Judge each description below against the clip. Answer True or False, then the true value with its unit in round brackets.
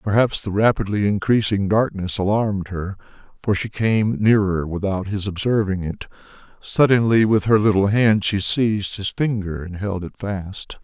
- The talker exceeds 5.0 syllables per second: False (4.6 syllables/s)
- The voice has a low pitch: True (100 Hz)